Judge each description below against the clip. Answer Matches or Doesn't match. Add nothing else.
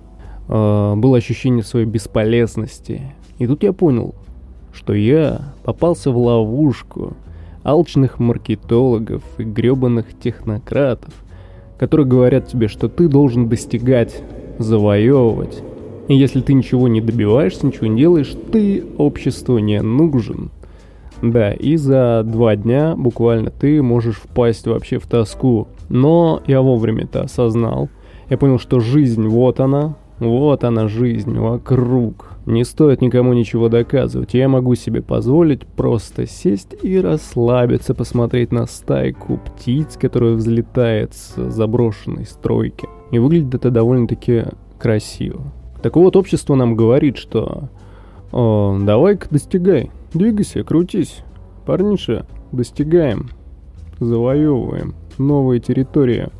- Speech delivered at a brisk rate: Doesn't match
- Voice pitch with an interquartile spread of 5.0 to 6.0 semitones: Doesn't match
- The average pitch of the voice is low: Matches